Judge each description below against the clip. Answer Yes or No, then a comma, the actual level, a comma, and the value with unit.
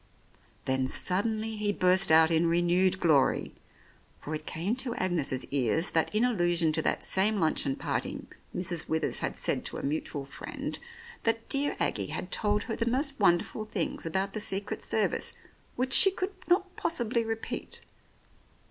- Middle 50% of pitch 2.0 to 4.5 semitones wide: No, wide, 5.6 semitones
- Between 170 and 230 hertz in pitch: Yes, high, 190 Hz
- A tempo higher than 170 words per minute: No, average, 160 wpm